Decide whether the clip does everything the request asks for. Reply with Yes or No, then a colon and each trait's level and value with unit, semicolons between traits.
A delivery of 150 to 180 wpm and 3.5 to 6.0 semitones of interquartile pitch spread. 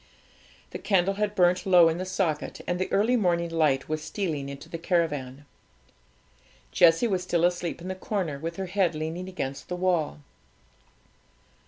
No: average, 165 wpm; average, 2.8 semitones